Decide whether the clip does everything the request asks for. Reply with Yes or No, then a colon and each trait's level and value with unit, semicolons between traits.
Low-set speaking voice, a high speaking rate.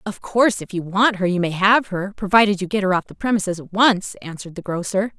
No: high, 195 Hz; fast, 255 wpm